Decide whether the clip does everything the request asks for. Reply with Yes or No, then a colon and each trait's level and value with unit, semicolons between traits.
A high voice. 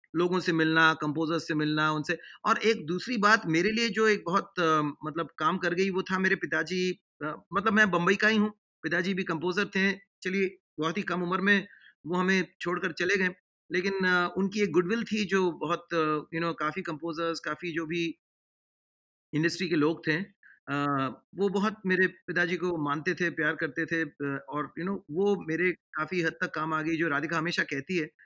No: medium, 175 Hz